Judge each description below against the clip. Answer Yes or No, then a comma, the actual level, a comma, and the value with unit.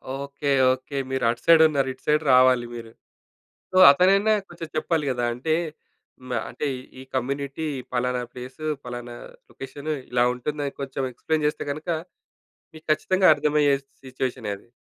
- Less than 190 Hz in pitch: Yes, medium, 140 Hz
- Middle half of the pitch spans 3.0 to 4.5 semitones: Yes, average, 3.5 semitones